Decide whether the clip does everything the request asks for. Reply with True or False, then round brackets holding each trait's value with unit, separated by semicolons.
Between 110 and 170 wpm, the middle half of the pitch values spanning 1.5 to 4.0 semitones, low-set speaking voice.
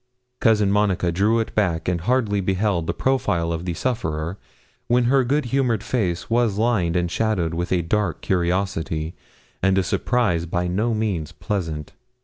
False (160 wpm; 4.7 semitones; 95 Hz)